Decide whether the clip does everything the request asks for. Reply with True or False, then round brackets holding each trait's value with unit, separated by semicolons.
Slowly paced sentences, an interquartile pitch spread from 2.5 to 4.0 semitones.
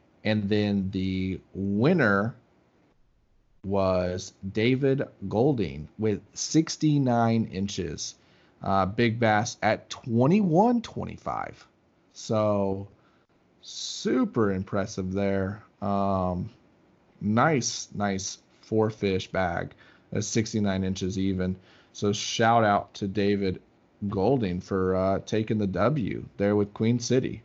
True (100 wpm; 3.2 semitones)